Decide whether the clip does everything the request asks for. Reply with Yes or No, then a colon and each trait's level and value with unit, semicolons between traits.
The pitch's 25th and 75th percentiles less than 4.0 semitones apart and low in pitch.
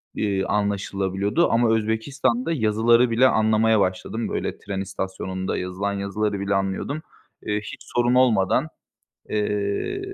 Yes: average, 2.9 semitones; low, 105 Hz